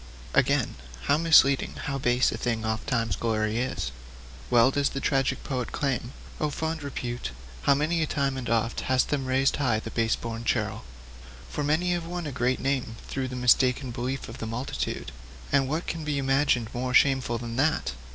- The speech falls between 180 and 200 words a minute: Yes, average, 190 wpm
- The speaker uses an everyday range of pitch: Yes, average, 3.1 semitones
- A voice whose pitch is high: No, low, 130 Hz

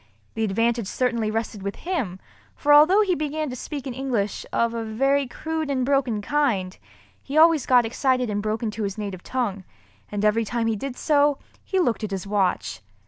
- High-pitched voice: Yes, high, 235 Hz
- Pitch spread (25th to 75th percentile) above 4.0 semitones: Yes, average, 5.1 semitones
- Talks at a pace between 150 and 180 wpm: No, average, 190 wpm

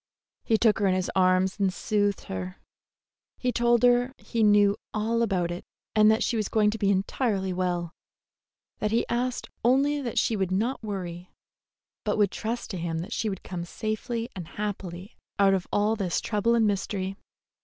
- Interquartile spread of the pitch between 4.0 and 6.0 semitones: No, average, 3.5 semitones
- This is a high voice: Yes, high, 205 Hz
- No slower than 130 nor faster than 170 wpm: No, average, 185 wpm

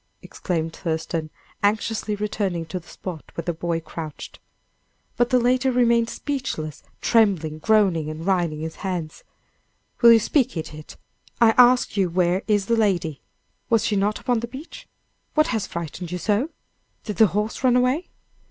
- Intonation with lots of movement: Yes, wide, 5.9 semitones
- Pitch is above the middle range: Yes, high, 200 Hz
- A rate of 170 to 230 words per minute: No, average, 160 wpm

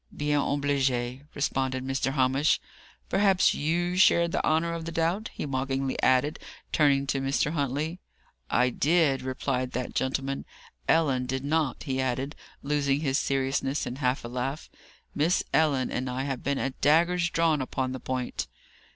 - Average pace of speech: Yes, average, 155 wpm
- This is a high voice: No, medium, 140 Hz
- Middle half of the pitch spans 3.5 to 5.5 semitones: No, average, 3.0 semitones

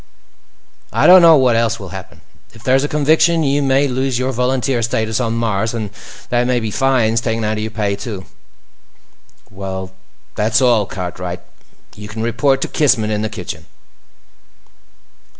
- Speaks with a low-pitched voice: Yes, low, 115 Hz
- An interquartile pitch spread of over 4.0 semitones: No, average, 3.7 semitones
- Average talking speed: Yes, average, 165 wpm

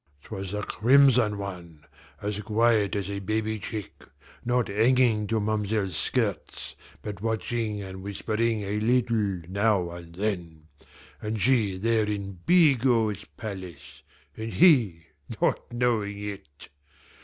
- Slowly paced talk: Yes, slow, 120 wpm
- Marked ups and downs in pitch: No, narrow, 2.6 semitones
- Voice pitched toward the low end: Yes, low, 105 Hz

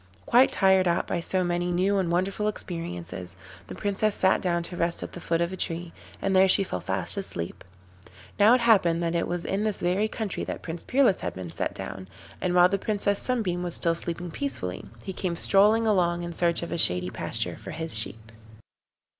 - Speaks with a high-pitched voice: No, medium, 175 Hz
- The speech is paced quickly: Yes, fast, 210 wpm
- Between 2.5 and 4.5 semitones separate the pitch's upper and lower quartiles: Yes, average, 2.9 semitones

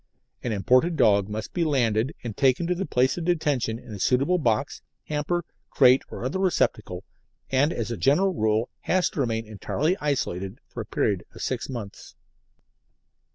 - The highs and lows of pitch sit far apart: Yes, wide, 5.9 semitones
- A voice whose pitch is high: No, low, 130 Hz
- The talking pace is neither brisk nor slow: Yes, average, 170 wpm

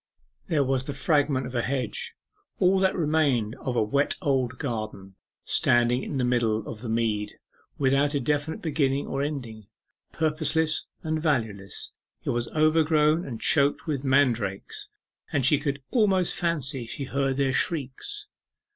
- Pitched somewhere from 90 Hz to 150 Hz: Yes, medium, 140 Hz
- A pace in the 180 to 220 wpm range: No, average, 150 wpm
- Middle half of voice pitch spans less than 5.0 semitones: Yes, average, 4.1 semitones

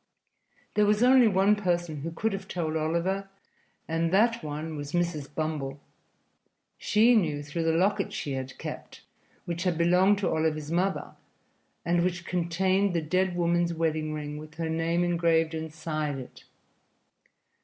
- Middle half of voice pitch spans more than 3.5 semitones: No, average, 3.0 semitones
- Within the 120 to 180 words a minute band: Yes, average, 150 wpm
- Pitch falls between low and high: Yes, medium, 170 Hz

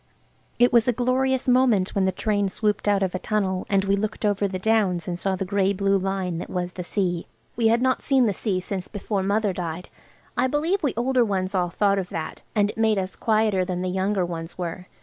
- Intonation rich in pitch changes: No, average, 3.1 semitones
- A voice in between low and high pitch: No, high, 200 Hz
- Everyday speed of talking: No, fast, 230 wpm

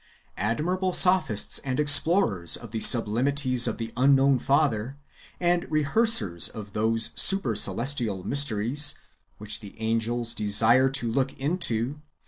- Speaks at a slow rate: Yes, slow, 120 wpm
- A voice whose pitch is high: No, low, 125 Hz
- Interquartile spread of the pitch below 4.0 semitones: No, average, 4.5 semitones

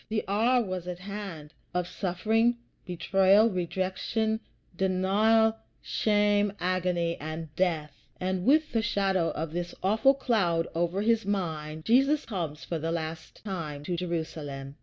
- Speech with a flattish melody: No, average, 4.4 semitones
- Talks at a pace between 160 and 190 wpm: No, slow, 135 wpm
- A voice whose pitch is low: No, medium, 185 Hz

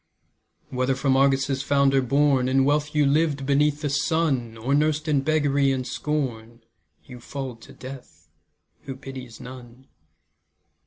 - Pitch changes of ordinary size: No, narrow, 2.2 semitones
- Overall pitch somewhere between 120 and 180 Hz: Yes, low, 135 Hz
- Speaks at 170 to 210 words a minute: No, average, 140 wpm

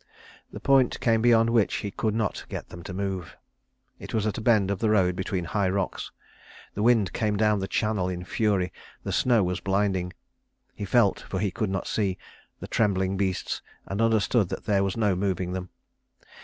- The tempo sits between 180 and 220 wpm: Yes, average, 195 wpm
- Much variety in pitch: No, average, 2.7 semitones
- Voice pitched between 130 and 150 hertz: No, low, 100 Hz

